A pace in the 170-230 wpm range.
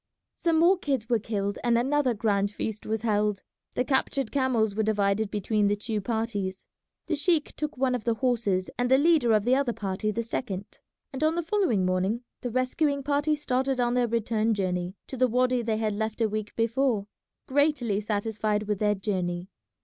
Yes: average, 190 wpm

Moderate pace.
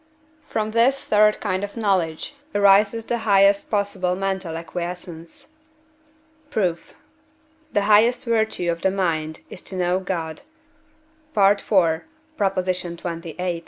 No: slow, 110 wpm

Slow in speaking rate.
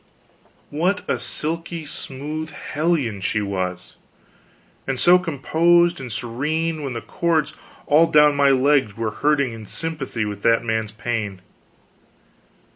Yes: slow, 125 wpm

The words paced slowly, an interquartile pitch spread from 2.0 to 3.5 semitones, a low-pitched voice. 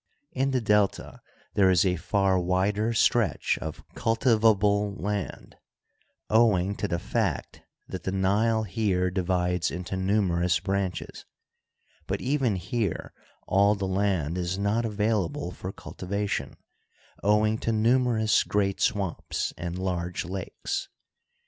Yes: slow, 120 wpm; average, 2.8 semitones; low, 100 Hz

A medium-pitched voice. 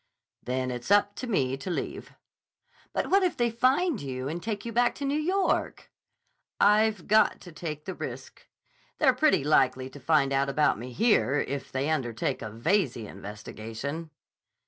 Yes: medium, 155 Hz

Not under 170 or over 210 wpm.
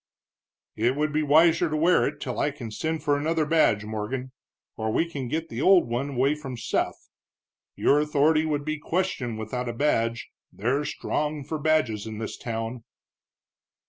Yes: average, 175 wpm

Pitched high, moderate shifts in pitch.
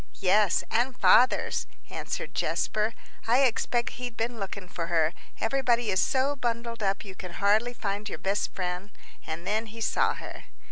Yes: high, 215 Hz; average, 3.7 semitones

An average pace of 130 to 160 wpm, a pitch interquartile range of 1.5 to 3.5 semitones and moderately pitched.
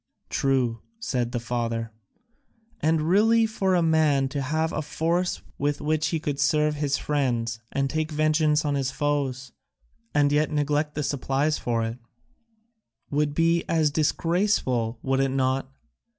Yes: average, 150 wpm; average, 2.8 semitones; medium, 145 Hz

